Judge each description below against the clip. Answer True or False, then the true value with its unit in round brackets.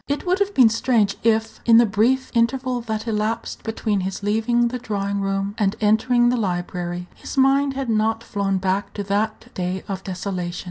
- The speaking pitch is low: False (220 Hz)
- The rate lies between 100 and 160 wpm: False (185 wpm)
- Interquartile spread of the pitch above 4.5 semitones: False (3.4 semitones)